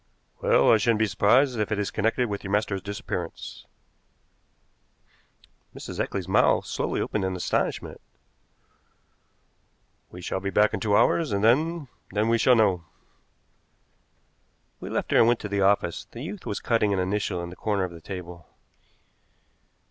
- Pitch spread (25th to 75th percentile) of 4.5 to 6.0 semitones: No, average, 3.2 semitones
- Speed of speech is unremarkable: Yes, average, 160 wpm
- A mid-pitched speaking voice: No, low, 105 Hz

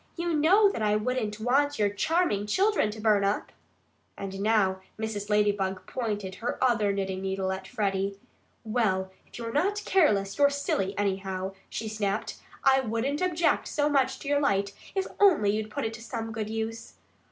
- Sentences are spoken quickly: No, average, 175 wpm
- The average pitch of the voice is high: Yes, high, 215 Hz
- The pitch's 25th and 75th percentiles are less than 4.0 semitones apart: No, average, 5.3 semitones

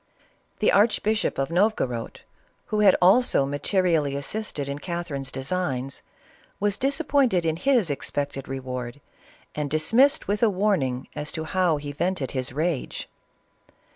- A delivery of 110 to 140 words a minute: Yes, slow, 135 wpm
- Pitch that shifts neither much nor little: No, wide, 6.8 semitones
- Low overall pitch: No, medium, 160 Hz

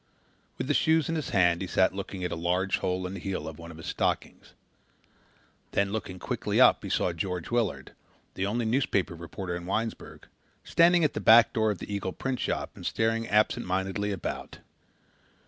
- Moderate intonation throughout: Yes, average, 3.9 semitones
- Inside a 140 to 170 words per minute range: No, average, 185 wpm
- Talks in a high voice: No, very low, 95 Hz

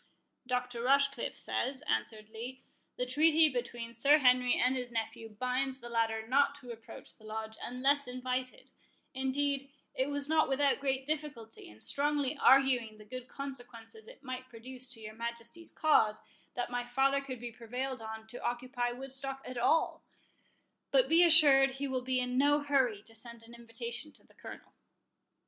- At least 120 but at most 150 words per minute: No, average, 165 wpm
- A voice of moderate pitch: No, very high, 255 Hz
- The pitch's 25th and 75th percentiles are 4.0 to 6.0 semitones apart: No, average, 2.8 semitones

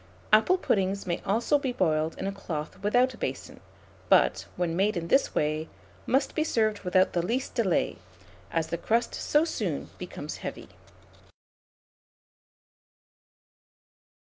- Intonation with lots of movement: Yes, wide, 6.3 semitones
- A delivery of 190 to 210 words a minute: No, slow, 135 wpm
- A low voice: No, high, 200 Hz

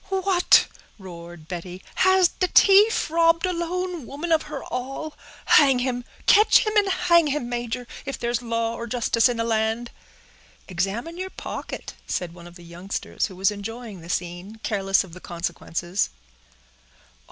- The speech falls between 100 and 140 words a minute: No, average, 160 wpm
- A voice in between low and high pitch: No, high, 240 Hz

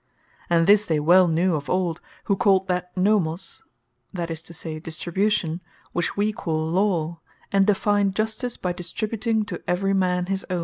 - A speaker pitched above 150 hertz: Yes, medium, 185 Hz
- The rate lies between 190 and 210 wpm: No, average, 170 wpm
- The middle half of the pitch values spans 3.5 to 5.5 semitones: No, average, 3.1 semitones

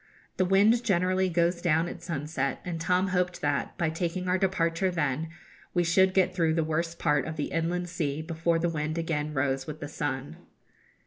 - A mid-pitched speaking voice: Yes, medium, 165 Hz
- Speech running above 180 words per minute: Yes, average, 190 wpm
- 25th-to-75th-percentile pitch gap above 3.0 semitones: No, average, 2.7 semitones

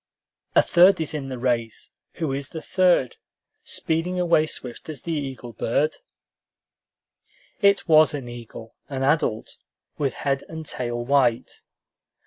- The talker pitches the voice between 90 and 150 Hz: Yes, medium, 140 Hz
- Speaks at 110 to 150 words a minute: Yes, slow, 135 wpm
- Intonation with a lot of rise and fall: No, average, 4.6 semitones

